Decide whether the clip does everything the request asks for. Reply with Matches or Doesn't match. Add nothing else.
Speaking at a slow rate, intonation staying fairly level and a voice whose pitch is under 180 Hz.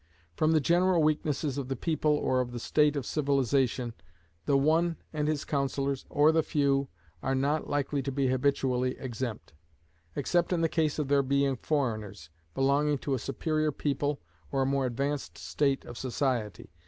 Doesn't match